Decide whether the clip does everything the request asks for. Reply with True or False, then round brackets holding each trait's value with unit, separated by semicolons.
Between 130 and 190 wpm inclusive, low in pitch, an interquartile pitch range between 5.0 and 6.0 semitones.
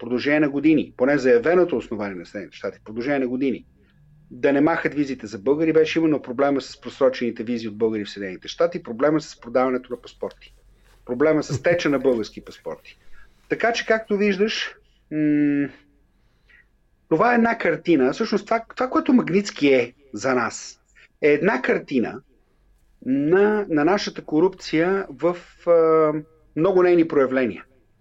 False (145 wpm; 150 Hz; 5.5 semitones)